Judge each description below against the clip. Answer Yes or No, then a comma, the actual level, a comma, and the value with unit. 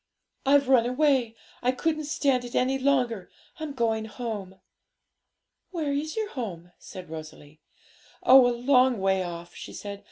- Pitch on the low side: No, high, 245 Hz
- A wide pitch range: Yes, wide, 6.0 semitones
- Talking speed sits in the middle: Yes, average, 150 wpm